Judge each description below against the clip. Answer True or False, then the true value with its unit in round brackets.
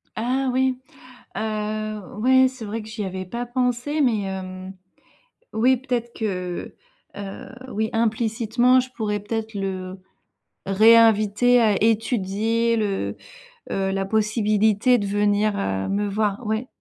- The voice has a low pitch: False (215 Hz)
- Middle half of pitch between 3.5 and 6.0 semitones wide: False (2.9 semitones)